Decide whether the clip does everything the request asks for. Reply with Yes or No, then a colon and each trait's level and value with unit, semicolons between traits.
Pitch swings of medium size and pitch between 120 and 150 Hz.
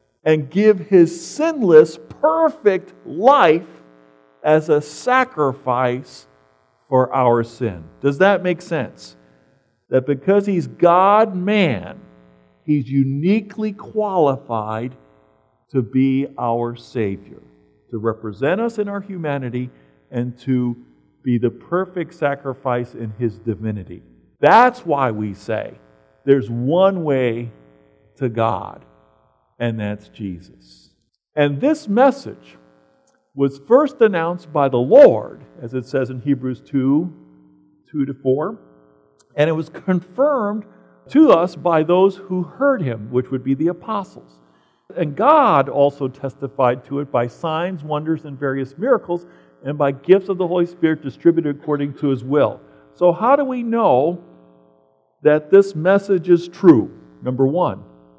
No: wide, 8.6 semitones; low, 135 Hz